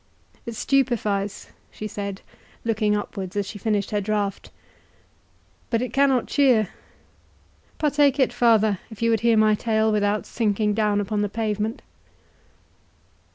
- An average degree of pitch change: No, narrow, 2.1 semitones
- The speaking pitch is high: Yes, high, 215 Hz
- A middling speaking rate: No, slow, 130 wpm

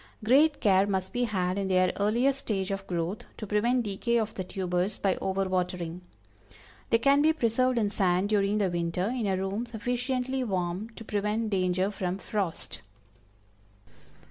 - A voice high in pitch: Yes, high, 200 Hz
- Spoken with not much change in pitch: No, average, 3.9 semitones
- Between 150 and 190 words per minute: Yes, average, 165 wpm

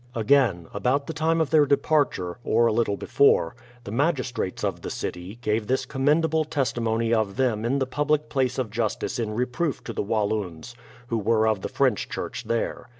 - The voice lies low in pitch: Yes, low, 120 Hz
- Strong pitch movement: No, average, 4.7 semitones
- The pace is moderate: Yes, average, 190 wpm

